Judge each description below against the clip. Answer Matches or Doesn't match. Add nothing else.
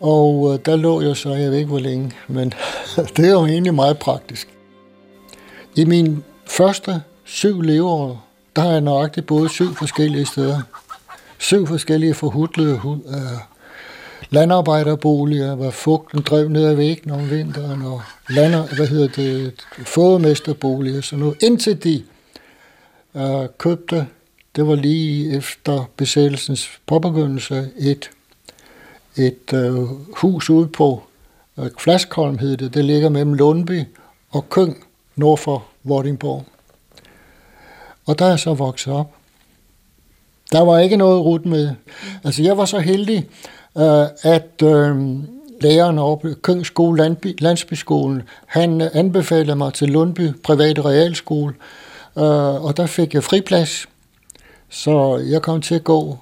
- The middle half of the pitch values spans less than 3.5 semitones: Matches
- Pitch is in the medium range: Matches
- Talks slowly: Matches